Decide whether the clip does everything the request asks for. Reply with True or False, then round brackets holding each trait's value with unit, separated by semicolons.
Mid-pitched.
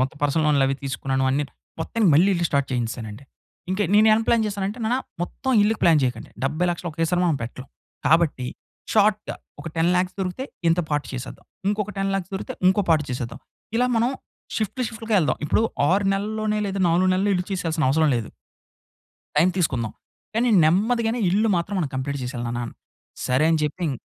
True (175 Hz)